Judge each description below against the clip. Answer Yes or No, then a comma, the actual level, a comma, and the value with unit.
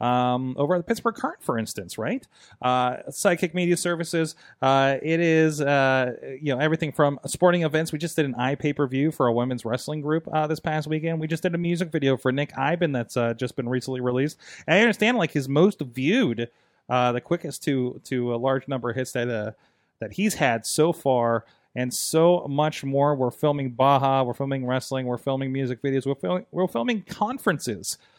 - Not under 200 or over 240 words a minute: Yes, fast, 205 wpm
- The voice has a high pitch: No, medium, 140 Hz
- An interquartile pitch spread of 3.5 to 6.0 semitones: Yes, average, 4.2 semitones